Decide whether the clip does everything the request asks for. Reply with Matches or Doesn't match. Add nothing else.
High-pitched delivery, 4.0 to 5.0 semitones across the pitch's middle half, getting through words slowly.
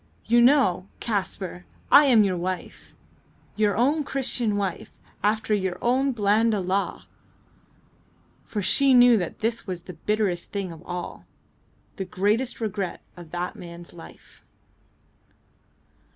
Matches